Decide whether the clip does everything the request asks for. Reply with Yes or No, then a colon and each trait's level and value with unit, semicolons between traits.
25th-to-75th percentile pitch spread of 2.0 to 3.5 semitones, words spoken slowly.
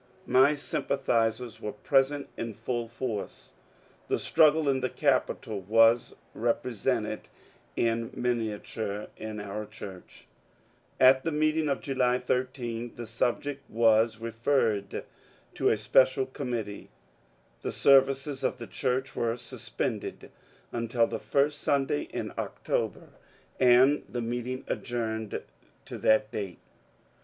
Yes: average, 3.0 semitones; slow, 120 wpm